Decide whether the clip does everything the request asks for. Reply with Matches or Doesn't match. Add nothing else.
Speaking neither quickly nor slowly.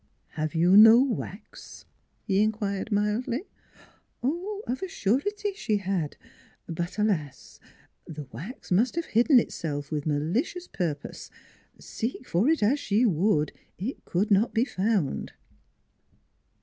Doesn't match